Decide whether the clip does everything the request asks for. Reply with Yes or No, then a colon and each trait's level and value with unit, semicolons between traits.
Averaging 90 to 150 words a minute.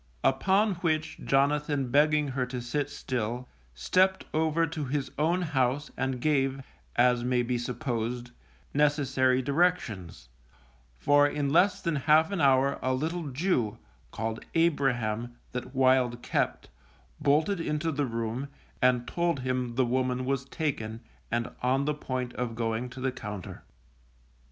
Yes: average, 140 wpm